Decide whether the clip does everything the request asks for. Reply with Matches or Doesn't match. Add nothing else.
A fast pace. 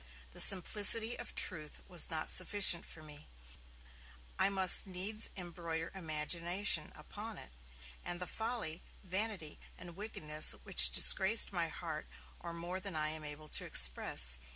Doesn't match